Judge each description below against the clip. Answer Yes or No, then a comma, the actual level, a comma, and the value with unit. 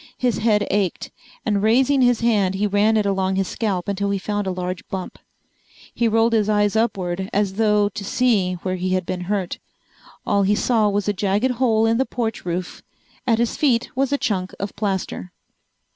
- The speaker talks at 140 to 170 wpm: No, average, 195 wpm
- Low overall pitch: No, high, 205 Hz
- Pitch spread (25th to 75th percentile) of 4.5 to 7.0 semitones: No, average, 2.9 semitones